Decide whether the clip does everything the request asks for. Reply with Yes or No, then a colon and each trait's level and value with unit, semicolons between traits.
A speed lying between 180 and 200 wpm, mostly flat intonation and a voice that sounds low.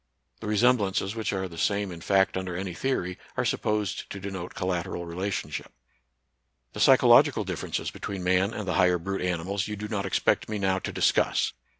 Yes: average, 185 wpm; narrow, 2.1 semitones; very low, 95 Hz